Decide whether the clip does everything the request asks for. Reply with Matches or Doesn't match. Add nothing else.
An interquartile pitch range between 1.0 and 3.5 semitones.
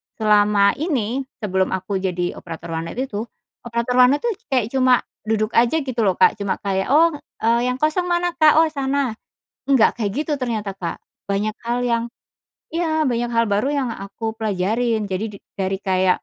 Doesn't match